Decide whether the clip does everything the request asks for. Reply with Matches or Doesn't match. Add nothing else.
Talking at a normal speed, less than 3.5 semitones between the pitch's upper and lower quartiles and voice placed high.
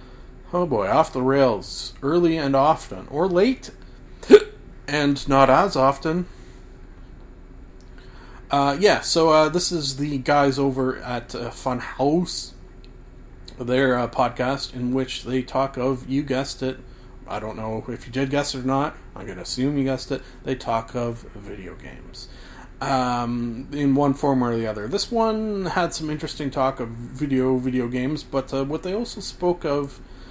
Doesn't match